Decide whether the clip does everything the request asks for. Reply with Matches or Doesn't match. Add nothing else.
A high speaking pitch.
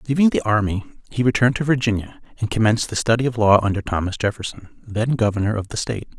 Doesn't match